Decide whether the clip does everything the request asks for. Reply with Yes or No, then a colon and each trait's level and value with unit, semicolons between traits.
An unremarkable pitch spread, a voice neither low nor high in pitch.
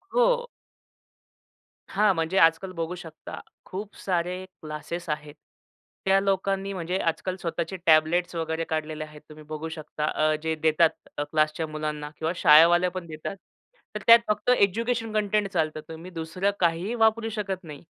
Yes: average, 3.8 semitones; medium, 170 Hz